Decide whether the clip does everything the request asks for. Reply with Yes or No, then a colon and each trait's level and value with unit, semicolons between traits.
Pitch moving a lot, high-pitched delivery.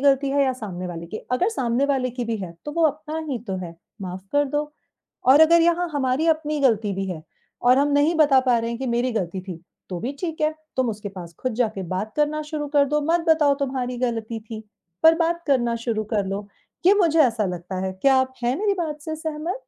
Yes: wide, 5.7 semitones; very high, 260 Hz